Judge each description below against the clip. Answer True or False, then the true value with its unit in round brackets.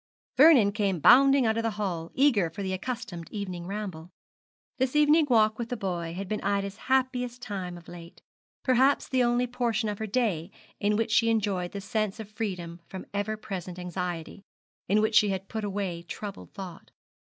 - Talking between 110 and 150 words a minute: False (185 wpm)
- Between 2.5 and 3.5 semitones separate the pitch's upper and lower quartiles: False (4.2 semitones)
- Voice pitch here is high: True (205 Hz)